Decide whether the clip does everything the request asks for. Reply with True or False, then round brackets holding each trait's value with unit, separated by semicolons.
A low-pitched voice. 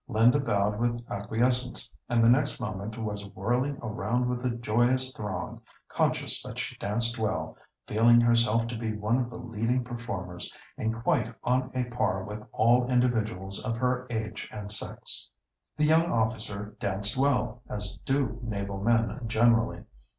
True (115 Hz)